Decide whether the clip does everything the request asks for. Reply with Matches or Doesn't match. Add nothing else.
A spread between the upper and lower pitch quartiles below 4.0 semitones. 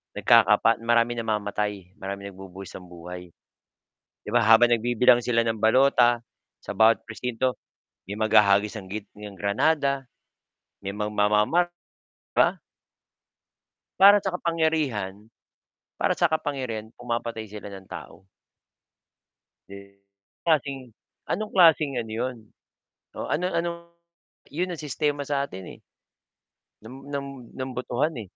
Doesn't match